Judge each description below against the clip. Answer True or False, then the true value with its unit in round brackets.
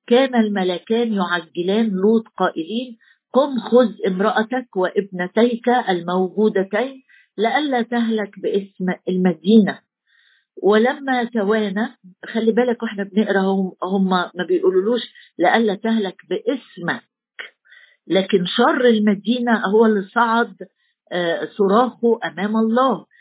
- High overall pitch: True (220 Hz)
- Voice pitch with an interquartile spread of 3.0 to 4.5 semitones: True (4.0 semitones)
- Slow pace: False (90 wpm)